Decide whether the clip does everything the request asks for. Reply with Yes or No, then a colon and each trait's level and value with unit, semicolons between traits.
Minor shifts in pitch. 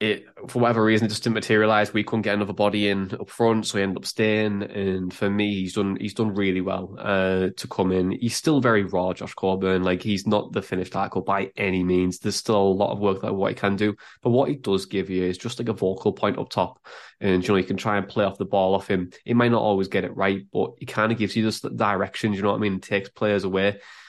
Yes: narrow, 2.0 semitones